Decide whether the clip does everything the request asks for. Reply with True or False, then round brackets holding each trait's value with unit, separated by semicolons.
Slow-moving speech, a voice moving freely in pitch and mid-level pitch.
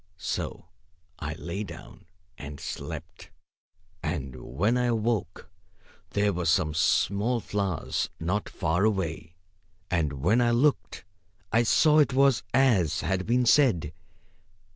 False (120 wpm; 6.5 semitones; 100 Hz)